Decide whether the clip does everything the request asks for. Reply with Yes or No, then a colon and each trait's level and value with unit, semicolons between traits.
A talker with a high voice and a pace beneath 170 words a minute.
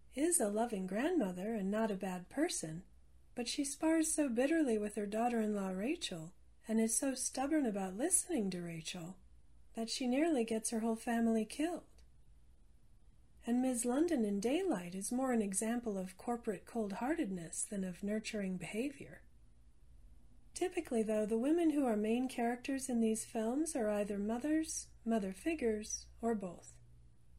Yes: high, 225 Hz; average, 155 wpm